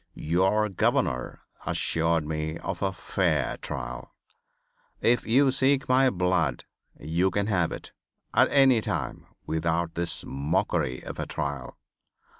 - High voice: No, very low, 85 Hz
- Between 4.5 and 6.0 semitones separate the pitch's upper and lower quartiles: Yes, wide, 5.4 semitones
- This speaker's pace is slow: Yes, slow, 125 wpm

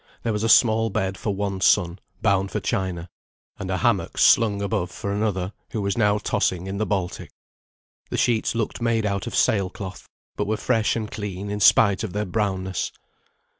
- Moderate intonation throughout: No, narrow, 2.3 semitones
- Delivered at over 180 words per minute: Yes, average, 190 wpm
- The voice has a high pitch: No, low, 100 Hz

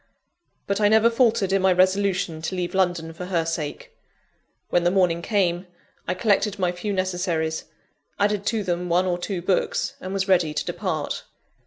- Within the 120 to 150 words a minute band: No, average, 175 wpm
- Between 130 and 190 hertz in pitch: Yes, medium, 185 Hz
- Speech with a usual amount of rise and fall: No, narrow, 2.2 semitones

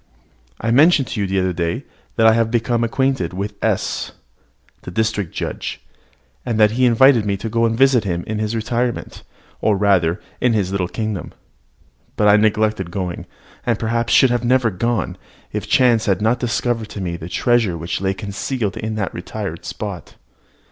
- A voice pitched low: Yes, low, 110 Hz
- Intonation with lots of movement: No, average, 3.5 semitones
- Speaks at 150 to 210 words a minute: Yes, average, 185 wpm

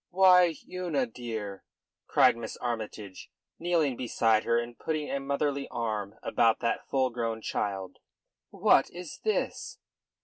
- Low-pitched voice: Yes, low, 120 Hz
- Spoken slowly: Yes, slow, 130 wpm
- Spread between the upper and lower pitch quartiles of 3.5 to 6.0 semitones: Yes, average, 5.1 semitones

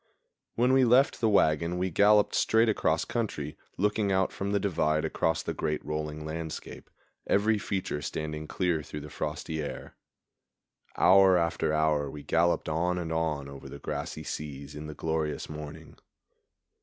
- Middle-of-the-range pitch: No, very low, 80 Hz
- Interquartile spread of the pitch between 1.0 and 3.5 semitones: No, average, 4.2 semitones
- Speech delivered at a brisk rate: No, average, 155 wpm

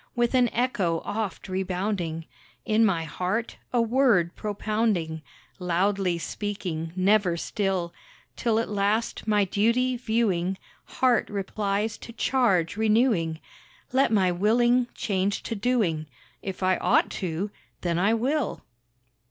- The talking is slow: Yes, slow, 120 wpm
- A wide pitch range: No, average, 4.0 semitones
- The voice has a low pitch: No, high, 205 Hz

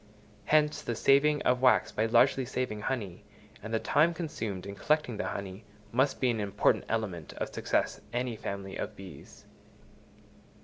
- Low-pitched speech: Yes, low, 115 Hz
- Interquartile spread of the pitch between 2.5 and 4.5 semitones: No, average, 5.2 semitones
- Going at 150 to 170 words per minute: Yes, average, 160 wpm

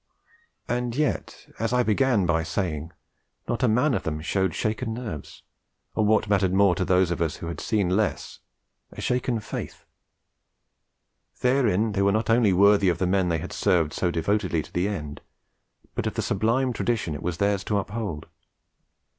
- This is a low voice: Yes, low, 100 Hz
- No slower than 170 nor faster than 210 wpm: Yes, average, 180 wpm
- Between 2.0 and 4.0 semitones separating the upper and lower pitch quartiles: No, average, 4.4 semitones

